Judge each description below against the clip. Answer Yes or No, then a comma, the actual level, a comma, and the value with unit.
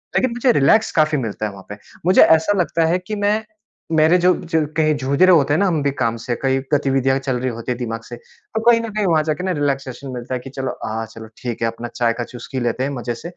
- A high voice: No, low, 135 Hz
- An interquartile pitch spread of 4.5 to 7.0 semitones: Yes, average, 5.2 semitones